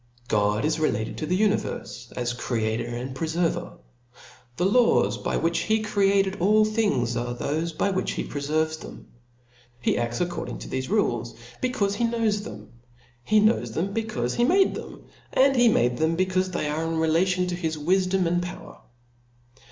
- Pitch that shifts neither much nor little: No, wide, 7.6 semitones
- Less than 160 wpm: No, average, 165 wpm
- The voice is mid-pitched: Yes, medium, 170 Hz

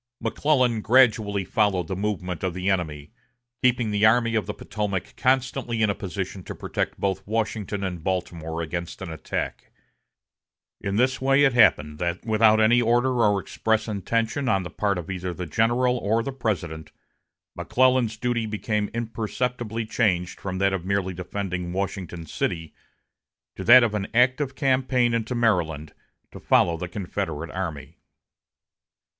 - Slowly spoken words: No, average, 150 wpm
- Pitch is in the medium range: No, low, 105 Hz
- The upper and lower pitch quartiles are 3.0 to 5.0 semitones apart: Yes, average, 4.5 semitones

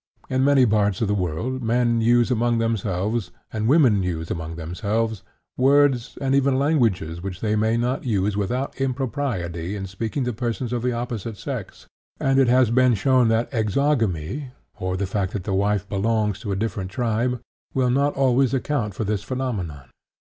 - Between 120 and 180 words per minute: Yes, average, 175 wpm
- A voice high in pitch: No, low, 115 Hz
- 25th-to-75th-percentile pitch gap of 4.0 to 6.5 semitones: Yes, average, 4.5 semitones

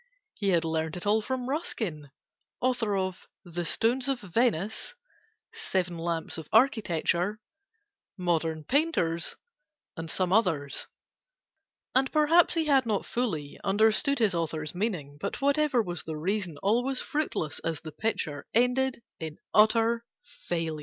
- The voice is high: Yes, high, 200 Hz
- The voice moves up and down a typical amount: No, wide, 7.2 semitones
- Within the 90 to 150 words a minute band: Yes, average, 140 wpm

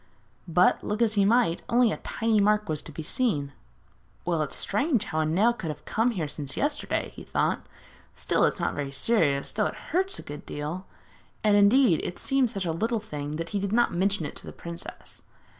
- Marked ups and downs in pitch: Yes, wide, 6.4 semitones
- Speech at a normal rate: No, fast, 215 wpm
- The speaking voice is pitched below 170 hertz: No, high, 200 Hz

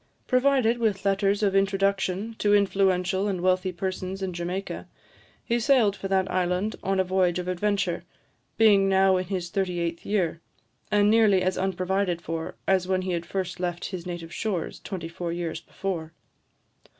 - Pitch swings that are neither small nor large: No, narrow, 1.8 semitones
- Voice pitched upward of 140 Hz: Yes, high, 190 Hz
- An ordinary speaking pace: Yes, average, 165 wpm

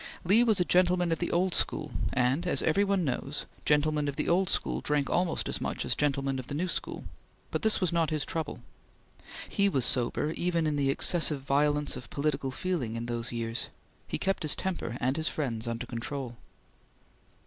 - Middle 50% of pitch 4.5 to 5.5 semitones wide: Yes, average, 4.8 semitones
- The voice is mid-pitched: Yes, medium, 150 Hz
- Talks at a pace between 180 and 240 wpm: Yes, average, 195 wpm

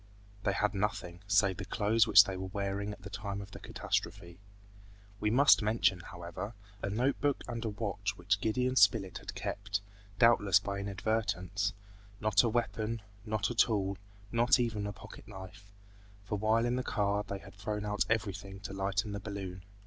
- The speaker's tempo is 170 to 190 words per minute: Yes, average, 180 wpm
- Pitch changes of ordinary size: No, narrow, 2.1 semitones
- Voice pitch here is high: No, low, 100 Hz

